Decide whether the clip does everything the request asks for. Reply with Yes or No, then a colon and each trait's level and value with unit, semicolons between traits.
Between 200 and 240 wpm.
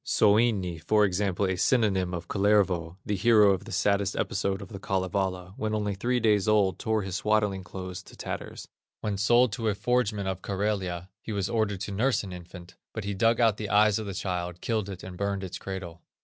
Yes: fast, 205 wpm